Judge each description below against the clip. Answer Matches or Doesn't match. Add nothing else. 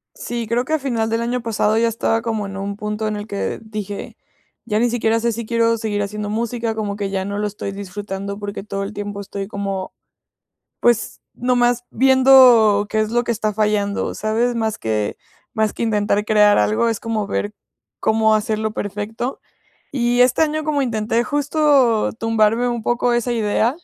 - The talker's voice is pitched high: Matches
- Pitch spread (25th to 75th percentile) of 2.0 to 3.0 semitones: Matches